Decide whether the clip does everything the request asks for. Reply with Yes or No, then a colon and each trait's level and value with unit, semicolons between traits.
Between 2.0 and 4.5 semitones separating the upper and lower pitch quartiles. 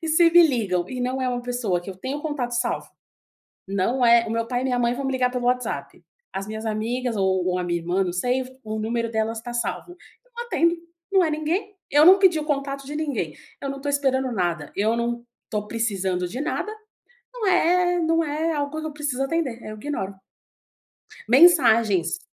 No: wide, 5.6 semitones